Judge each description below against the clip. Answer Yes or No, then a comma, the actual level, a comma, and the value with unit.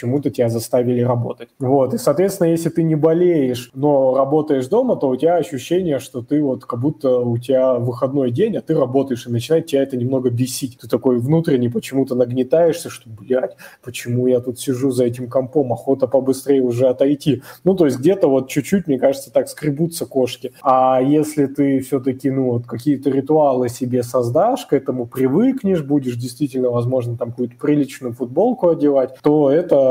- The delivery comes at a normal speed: No, fast, 175 wpm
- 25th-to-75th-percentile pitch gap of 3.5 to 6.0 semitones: No, average, 2.7 semitones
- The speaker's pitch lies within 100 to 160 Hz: Yes, low, 135 Hz